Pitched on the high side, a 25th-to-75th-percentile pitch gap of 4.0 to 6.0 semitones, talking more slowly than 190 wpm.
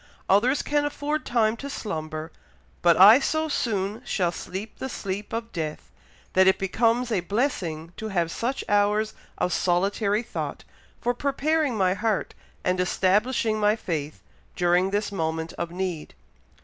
Yes: high, 205 Hz; average, 4.6 semitones; average, 150 wpm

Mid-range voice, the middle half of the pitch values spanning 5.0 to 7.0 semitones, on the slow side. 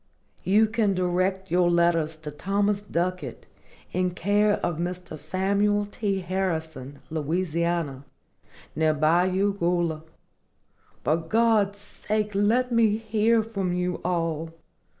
No: medium, 180 Hz; average, 3.7 semitones; slow, 110 wpm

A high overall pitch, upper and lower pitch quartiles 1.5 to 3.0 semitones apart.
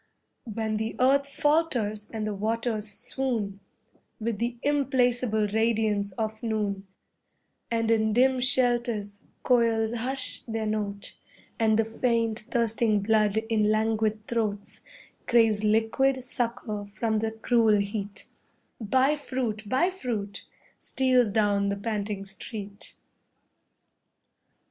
Yes: high, 220 Hz; narrow, 2.4 semitones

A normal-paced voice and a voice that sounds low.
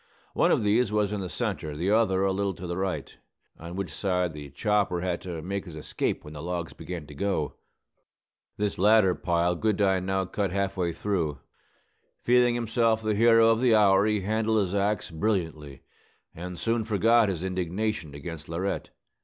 Yes: average, 180 wpm; very low, 95 Hz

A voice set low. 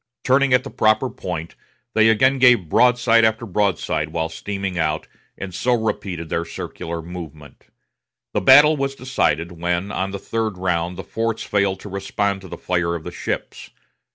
Yes: low, 100 Hz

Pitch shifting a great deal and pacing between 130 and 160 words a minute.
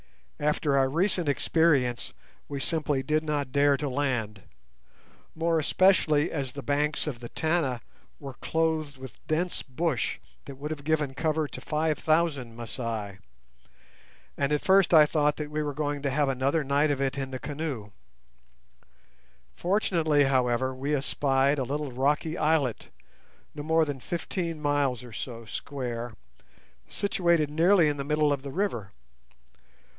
No: average, 2.8 semitones; average, 150 wpm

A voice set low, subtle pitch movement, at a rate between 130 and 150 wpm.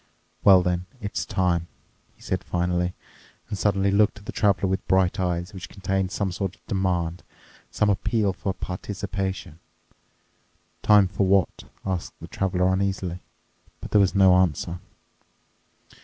Yes: very low, 95 Hz; narrow, 1.6 semitones; average, 140 wpm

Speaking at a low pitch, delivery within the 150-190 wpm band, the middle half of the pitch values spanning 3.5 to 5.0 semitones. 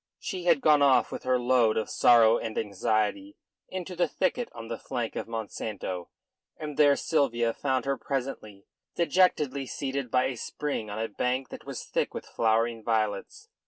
Yes: low, 125 Hz; average, 170 wpm; average, 4.3 semitones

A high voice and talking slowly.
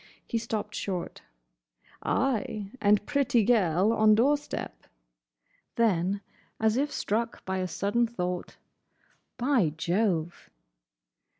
Yes: high, 215 Hz; slow, 105 wpm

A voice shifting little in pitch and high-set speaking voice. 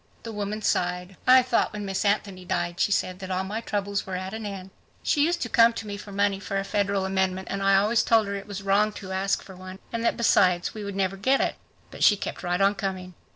Yes: narrow, 1.8 semitones; high, 195 Hz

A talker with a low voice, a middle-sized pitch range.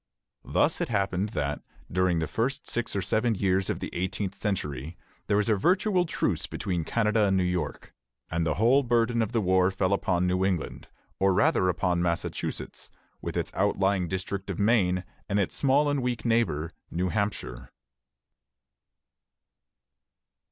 Yes: very low, 95 Hz; average, 3.8 semitones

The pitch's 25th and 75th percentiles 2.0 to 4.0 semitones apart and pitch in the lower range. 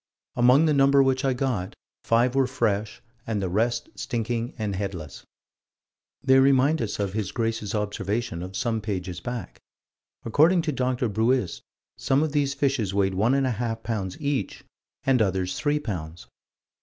No: average, 4.9 semitones; low, 115 Hz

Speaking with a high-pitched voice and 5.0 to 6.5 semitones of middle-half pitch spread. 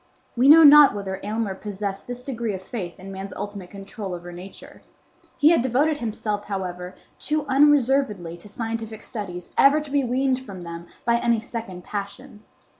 Yes: high, 215 Hz; average, 5.3 semitones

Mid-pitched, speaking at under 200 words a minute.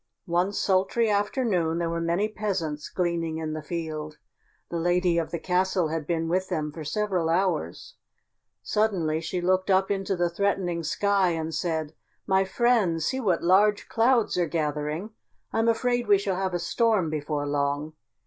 Yes: medium, 175 Hz; average, 165 wpm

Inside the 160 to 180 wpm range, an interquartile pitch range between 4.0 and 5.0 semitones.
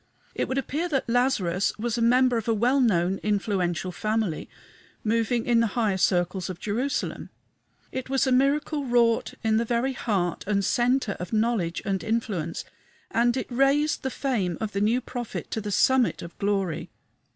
Yes: average, 175 wpm; average, 4.3 semitones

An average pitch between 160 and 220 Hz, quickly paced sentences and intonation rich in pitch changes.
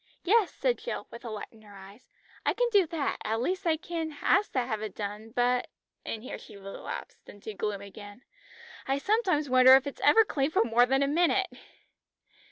No: very high, 255 Hz; fast, 210 wpm; wide, 7.6 semitones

